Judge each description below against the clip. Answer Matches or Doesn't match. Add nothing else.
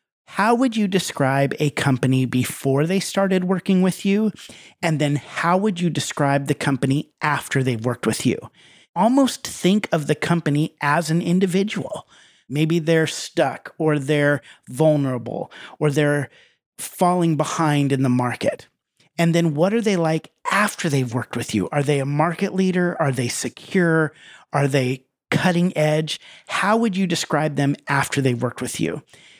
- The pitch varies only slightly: Doesn't match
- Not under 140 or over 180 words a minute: Matches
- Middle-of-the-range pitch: Matches